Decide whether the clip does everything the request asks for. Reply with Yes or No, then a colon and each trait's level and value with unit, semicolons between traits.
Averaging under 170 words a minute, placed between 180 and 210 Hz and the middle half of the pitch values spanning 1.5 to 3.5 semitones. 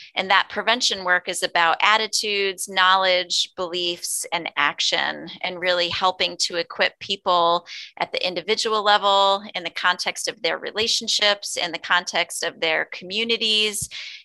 Yes: average, 140 wpm; medium, 185 Hz; average, 2.8 semitones